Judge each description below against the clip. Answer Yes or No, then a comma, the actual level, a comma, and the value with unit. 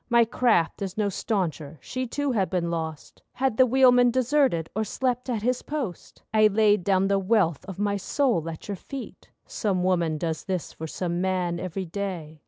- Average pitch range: No, wide, 5.8 semitones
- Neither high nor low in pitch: No, high, 200 Hz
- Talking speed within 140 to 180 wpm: No, average, 190 wpm